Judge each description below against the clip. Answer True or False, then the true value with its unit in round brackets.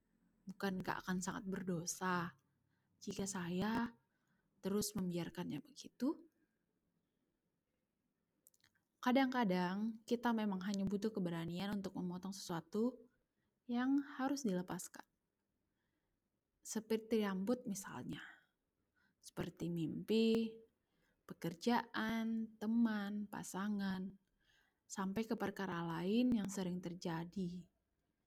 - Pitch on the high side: True (200 Hz)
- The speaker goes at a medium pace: False (80 wpm)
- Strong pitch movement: False (3.7 semitones)